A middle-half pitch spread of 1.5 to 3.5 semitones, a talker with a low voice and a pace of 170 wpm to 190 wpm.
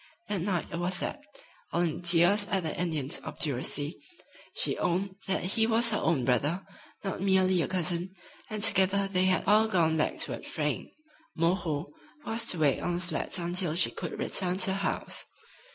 No: average, 2.7 semitones; medium, 180 Hz; average, 180 wpm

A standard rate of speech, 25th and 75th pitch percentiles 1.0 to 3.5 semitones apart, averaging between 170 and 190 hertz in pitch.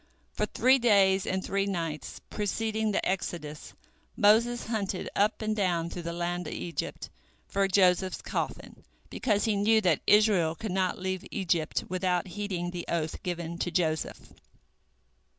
Yes: average, 150 wpm; average, 3.1 semitones; medium, 185 Hz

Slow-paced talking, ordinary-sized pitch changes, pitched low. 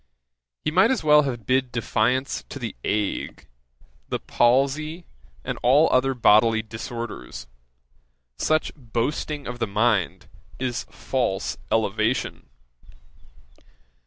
Yes: slow, 105 wpm; average, 3.8 semitones; low, 125 Hz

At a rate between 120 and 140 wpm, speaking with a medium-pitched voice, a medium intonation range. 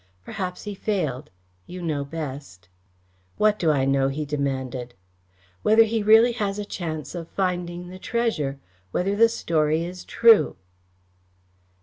No: slow, 135 wpm; medium, 175 Hz; wide, 6.3 semitones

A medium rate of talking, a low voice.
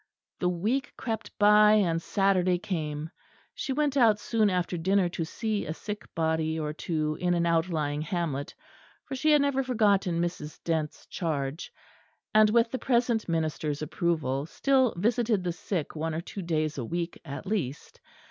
No: average, 165 wpm; medium, 175 Hz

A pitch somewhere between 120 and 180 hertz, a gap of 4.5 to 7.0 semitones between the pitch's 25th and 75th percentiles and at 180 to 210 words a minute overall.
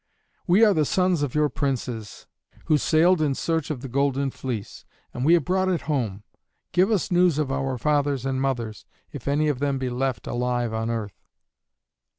No: medium, 140 Hz; average, 4.1 semitones; average, 185 wpm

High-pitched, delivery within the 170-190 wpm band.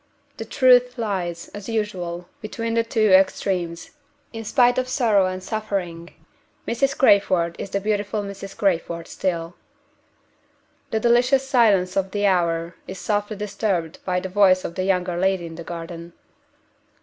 No: high, 195 Hz; average, 150 wpm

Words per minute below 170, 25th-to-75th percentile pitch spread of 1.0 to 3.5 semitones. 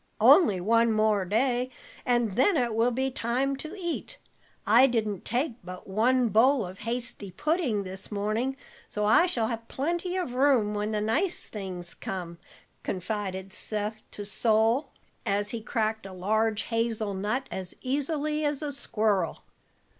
No: average, 155 wpm; average, 4.2 semitones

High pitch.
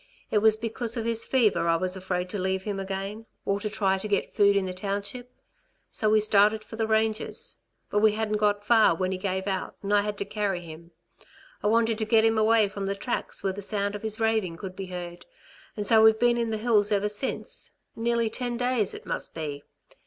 Yes: high, 210 Hz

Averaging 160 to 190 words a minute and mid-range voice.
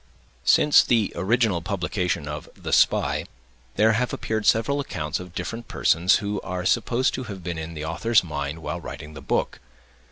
No: average, 170 wpm; very low, 90 Hz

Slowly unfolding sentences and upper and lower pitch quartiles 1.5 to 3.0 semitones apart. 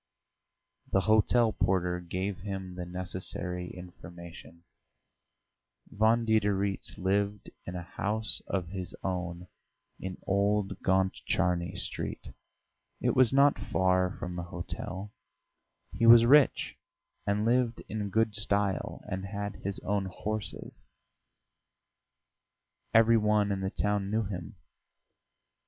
Yes: slow, 110 wpm; narrow, 2.6 semitones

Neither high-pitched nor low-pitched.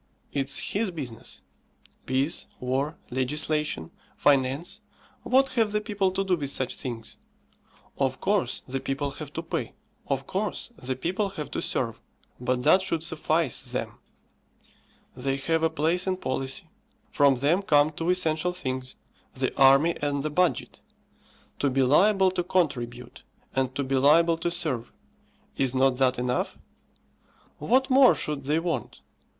Yes: medium, 150 Hz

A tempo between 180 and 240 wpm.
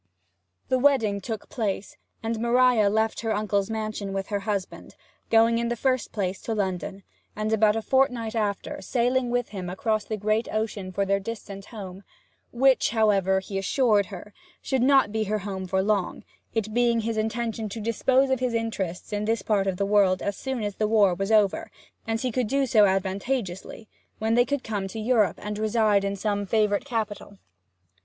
Yes: average, 190 wpm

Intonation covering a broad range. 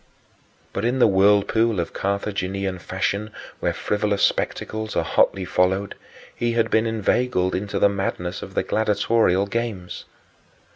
No: average, 2.7 semitones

